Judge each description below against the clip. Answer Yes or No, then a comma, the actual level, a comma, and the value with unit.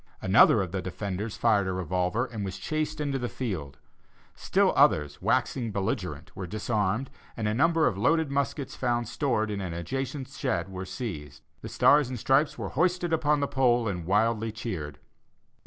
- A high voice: No, low, 110 Hz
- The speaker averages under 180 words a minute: Yes, average, 170 wpm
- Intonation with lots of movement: Yes, wide, 6.2 semitones